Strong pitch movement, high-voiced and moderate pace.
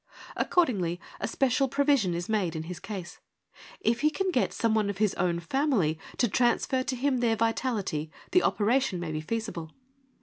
Yes: wide, 6.6 semitones; high, 220 Hz; average, 175 wpm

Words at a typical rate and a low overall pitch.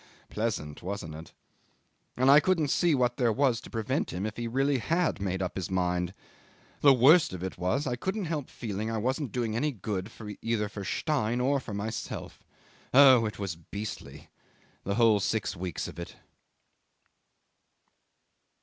Yes: average, 165 wpm; low, 115 Hz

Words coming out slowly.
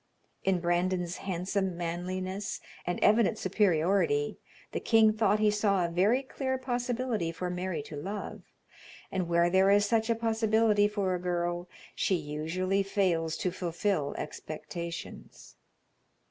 Yes: slow, 130 wpm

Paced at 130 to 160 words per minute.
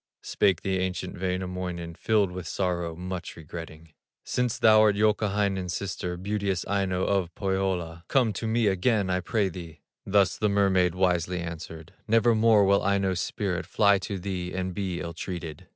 Yes: average, 150 wpm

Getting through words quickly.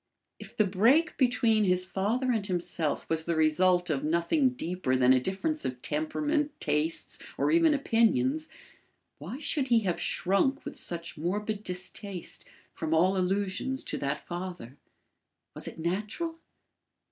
No: average, 145 wpm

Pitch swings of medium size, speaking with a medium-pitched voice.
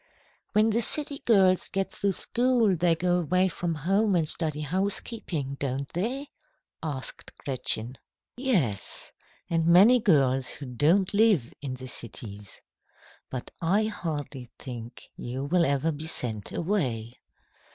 No: wide, 6.9 semitones; medium, 165 Hz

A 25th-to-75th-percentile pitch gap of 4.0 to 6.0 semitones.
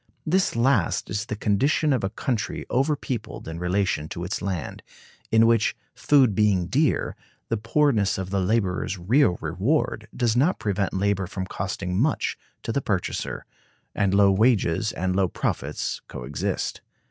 Yes: average, 4.5 semitones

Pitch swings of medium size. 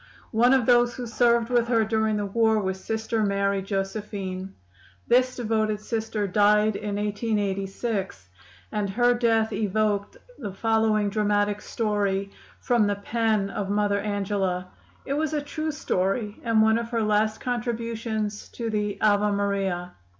No: narrow, 2.2 semitones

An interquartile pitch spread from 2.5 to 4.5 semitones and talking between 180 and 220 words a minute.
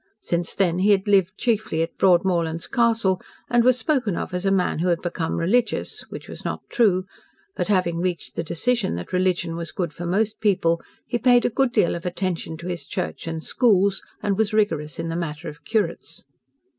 Yes: average, 4.1 semitones; average, 200 wpm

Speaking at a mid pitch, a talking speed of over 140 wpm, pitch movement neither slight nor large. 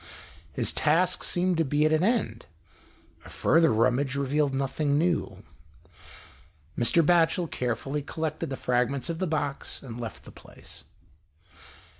No: medium, 150 Hz; slow, 135 wpm; average, 3.7 semitones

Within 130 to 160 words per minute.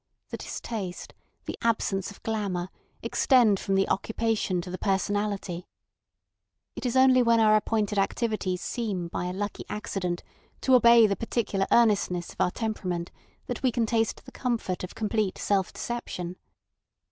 Yes: average, 150 wpm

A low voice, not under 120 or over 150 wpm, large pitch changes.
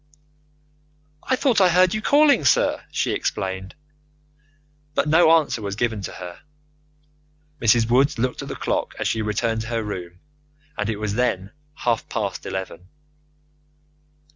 Yes: low, 115 Hz; average, 145 wpm; wide, 6.9 semitones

